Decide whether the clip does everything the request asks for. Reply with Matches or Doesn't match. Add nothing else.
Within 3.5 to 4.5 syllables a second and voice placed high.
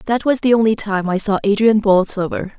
Doesn't match